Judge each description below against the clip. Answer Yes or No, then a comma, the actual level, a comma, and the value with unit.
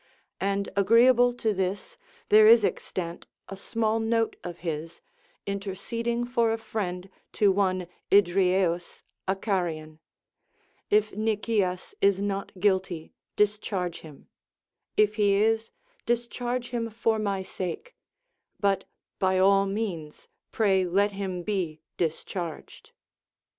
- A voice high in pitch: Yes, high, 200 Hz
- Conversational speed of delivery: No, slow, 115 wpm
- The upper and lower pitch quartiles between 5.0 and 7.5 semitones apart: No, average, 3.2 semitones